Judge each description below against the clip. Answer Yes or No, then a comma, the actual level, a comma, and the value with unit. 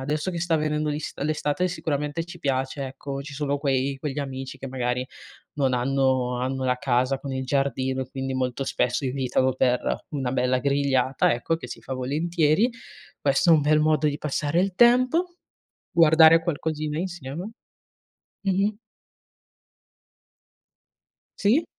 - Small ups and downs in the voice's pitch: No, average, 3.3 semitones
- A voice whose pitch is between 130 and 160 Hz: Yes, medium, 140 Hz